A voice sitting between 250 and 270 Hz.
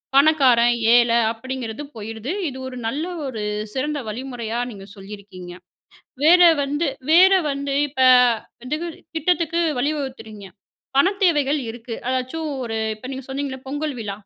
Yes: very high, 260 Hz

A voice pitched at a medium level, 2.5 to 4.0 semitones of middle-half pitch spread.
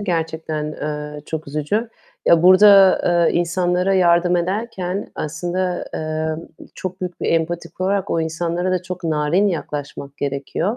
Yes: medium, 175 Hz; average, 2.8 semitones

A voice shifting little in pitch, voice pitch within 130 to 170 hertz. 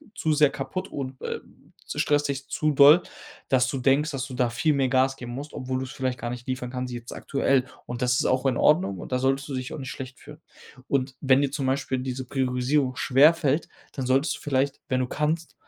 Yes: narrow, 1.9 semitones; low, 135 Hz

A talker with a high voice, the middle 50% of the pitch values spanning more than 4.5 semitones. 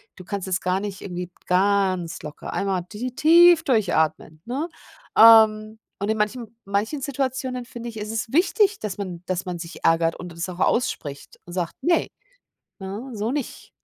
Yes: high, 205 Hz; average, 5.2 semitones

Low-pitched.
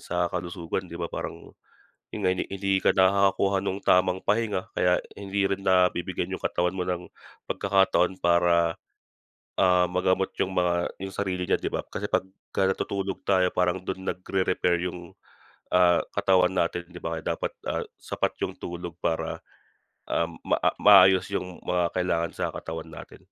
Yes: very low, 90 Hz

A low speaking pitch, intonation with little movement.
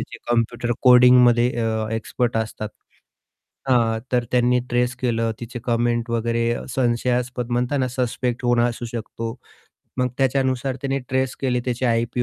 Yes: low, 120 Hz; narrow, 1.2 semitones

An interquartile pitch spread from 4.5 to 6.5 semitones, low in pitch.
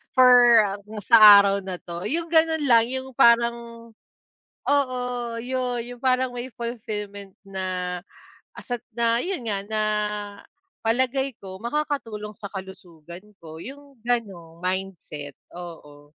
No: average, 5.1 semitones; high, 230 Hz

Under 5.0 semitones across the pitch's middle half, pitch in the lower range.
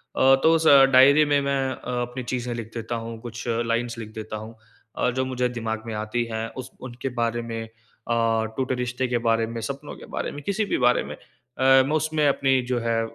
Yes: narrow, 2.6 semitones; low, 120 Hz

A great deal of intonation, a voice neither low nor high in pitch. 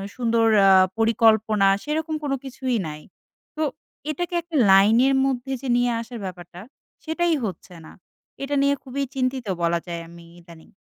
No: wide, 6.1 semitones; high, 240 Hz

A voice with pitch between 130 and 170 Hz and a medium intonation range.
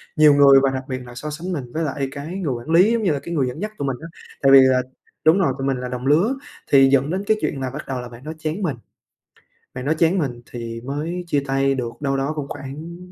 Yes: medium, 140 Hz; average, 3.3 semitones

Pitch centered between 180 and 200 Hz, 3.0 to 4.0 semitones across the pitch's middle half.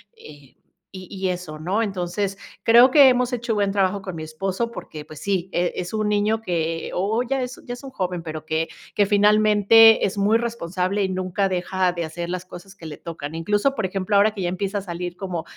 Yes: high, 190 Hz; average, 3.3 semitones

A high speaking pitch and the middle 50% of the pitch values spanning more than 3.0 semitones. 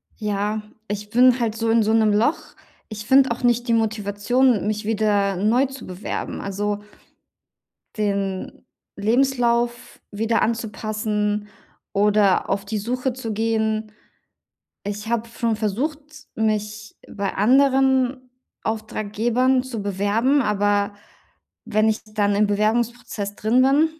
No: high, 220 Hz; narrow, 2.6 semitones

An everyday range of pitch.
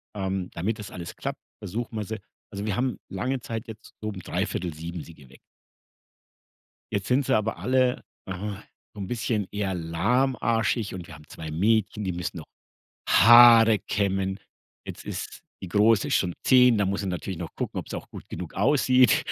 Yes: average, 4.0 semitones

